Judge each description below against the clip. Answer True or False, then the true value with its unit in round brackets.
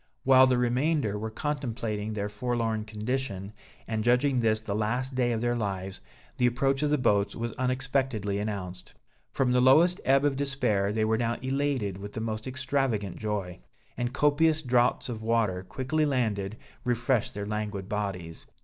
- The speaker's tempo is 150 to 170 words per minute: True (165 wpm)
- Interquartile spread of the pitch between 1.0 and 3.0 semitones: False (4.0 semitones)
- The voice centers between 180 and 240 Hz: False (115 Hz)